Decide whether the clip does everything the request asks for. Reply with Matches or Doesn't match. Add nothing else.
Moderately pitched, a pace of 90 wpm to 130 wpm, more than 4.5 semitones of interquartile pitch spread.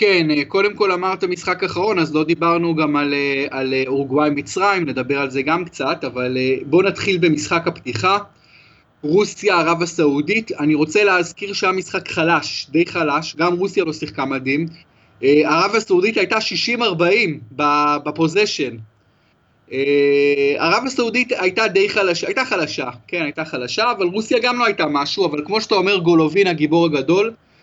Doesn't match